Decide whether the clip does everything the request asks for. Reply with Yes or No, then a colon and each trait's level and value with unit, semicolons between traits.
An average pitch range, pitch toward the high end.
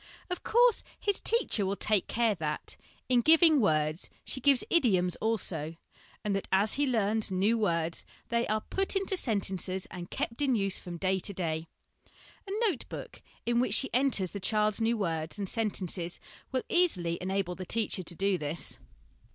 Yes: average, 4.9 semitones; high, 205 Hz